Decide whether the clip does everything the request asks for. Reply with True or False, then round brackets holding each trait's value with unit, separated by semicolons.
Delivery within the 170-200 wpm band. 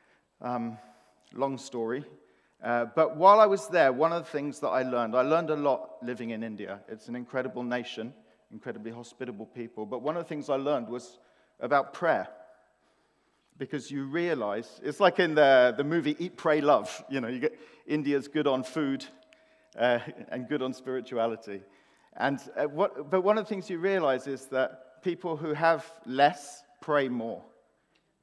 True (175 wpm)